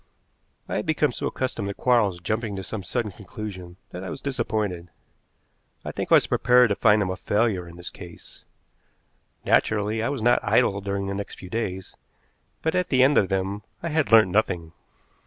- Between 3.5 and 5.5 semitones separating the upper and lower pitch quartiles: Yes, average, 4.0 semitones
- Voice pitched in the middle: No, low, 105 Hz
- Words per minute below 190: No, average, 195 wpm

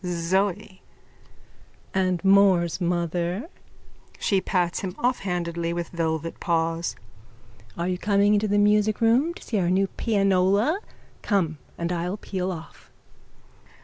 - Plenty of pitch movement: No, average, 2.9 semitones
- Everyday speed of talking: No, slow, 115 wpm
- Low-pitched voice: No, medium, 185 Hz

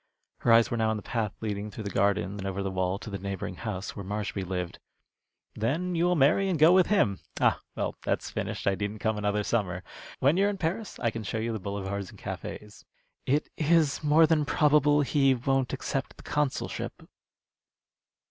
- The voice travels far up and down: Yes, wide, 6.8 semitones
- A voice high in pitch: No, low, 110 Hz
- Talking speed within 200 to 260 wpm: Yes, fast, 205 wpm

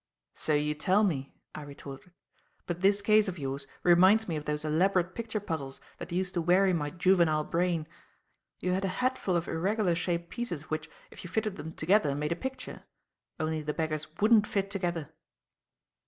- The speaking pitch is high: No, medium, 175 Hz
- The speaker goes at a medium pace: Yes, average, 180 wpm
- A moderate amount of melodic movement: Yes, average, 4.1 semitones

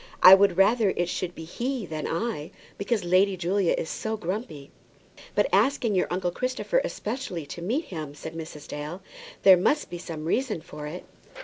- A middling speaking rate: Yes, average, 180 wpm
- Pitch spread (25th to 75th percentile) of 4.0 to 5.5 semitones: Yes, average, 5.1 semitones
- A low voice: No, medium, 185 Hz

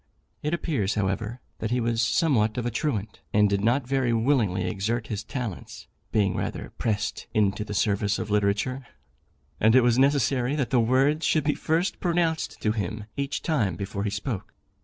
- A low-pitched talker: Yes, low, 115 Hz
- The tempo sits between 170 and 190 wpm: Yes, average, 180 wpm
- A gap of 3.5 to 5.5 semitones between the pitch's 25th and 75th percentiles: Yes, average, 4.5 semitones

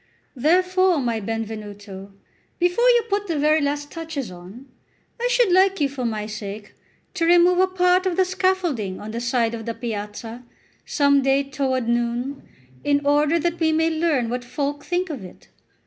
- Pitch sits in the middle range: No, very high, 280 Hz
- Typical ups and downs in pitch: No, wide, 7.2 semitones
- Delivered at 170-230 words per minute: Yes, average, 175 wpm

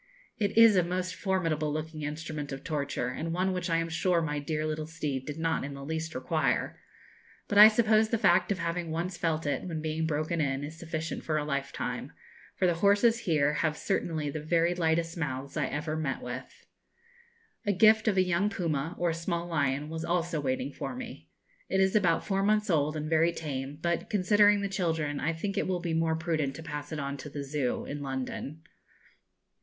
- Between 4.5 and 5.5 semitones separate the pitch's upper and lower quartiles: No, average, 3.3 semitones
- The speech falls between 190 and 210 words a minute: Yes, fast, 205 wpm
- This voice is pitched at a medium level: Yes, medium, 160 Hz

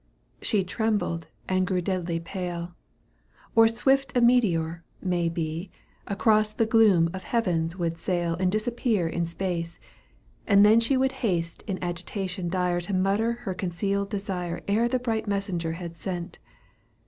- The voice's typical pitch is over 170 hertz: Yes, medium, 185 Hz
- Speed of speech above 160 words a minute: No, average, 145 wpm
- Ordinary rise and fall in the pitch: Yes, average, 4.2 semitones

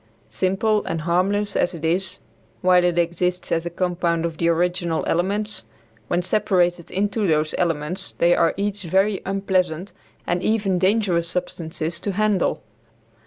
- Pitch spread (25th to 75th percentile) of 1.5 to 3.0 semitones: Yes, narrow, 2.4 semitones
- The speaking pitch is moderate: Yes, medium, 180 Hz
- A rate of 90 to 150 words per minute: Yes, average, 145 wpm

